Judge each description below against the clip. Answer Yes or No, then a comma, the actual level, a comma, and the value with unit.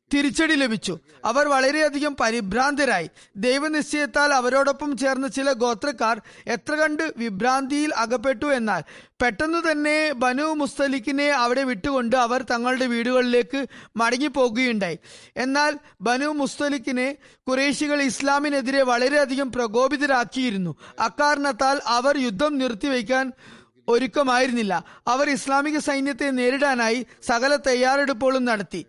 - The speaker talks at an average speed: Yes, average, 90 wpm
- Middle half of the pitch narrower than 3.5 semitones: Yes, average, 2.8 semitones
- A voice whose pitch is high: Yes, very high, 265 Hz